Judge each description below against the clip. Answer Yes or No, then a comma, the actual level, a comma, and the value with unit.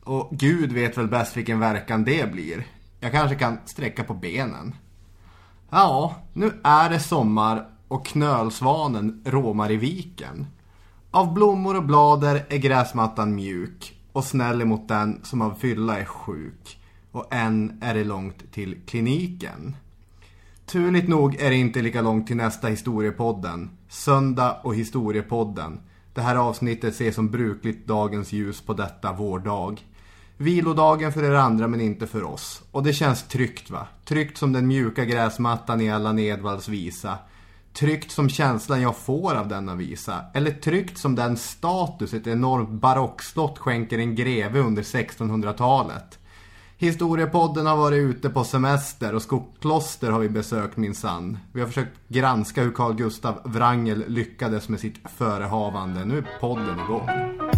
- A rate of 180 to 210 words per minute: No, average, 150 wpm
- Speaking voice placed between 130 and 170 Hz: No, low, 115 Hz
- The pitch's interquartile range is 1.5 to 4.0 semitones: No, average, 4.4 semitones